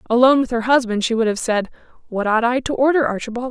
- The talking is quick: Yes, fast, 240 wpm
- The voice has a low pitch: No, high, 240 Hz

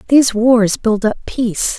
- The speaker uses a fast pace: No, average, 170 wpm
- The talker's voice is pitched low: No, high, 230 Hz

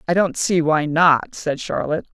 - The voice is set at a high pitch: No, medium, 160 Hz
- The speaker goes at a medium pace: Yes, average, 190 wpm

